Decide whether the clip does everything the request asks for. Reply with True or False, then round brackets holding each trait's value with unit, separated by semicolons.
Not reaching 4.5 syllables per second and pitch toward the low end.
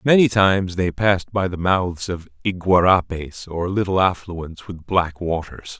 True (4.3 syllables/s; 90 Hz)